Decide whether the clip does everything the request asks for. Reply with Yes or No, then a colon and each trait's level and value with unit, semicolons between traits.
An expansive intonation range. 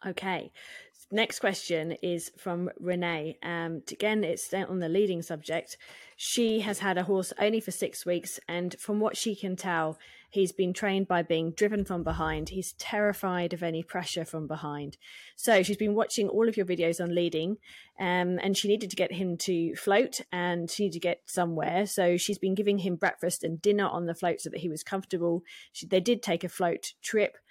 No: average, 2.9 semitones